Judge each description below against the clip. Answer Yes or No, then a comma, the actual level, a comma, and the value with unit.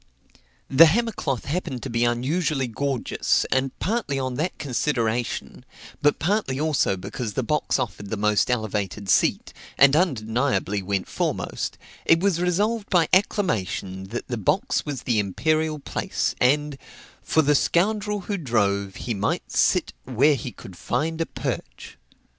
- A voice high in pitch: No, low, 135 Hz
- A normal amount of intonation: No, wide, 6.7 semitones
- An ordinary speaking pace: Yes, average, 145 wpm